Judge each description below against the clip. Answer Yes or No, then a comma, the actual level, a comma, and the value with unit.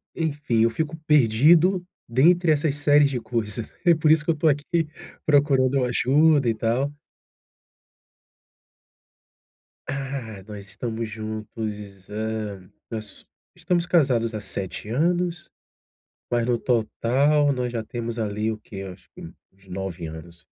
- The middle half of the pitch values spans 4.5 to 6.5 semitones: Yes, wide, 5.4 semitones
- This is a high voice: No, low, 120 Hz